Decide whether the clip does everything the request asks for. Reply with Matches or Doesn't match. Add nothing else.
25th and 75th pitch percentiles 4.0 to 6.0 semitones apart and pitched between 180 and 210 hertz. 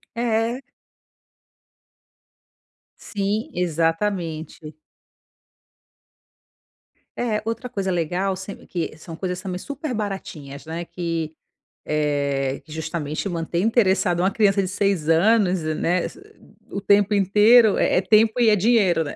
Matches